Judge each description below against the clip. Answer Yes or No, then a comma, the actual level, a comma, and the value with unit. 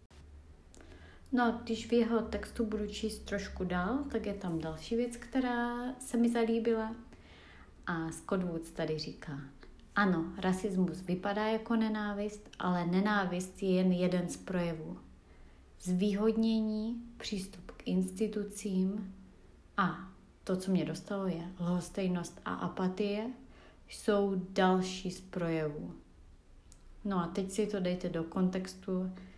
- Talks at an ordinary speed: Yes, average, 125 wpm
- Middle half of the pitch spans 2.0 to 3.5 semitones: No, average, 4.2 semitones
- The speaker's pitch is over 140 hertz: Yes, medium, 185 Hz